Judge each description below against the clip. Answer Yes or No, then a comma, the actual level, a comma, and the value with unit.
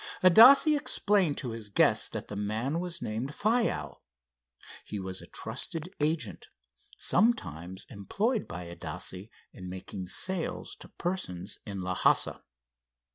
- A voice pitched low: Yes, low, 115 Hz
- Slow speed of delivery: Yes, slow, 125 wpm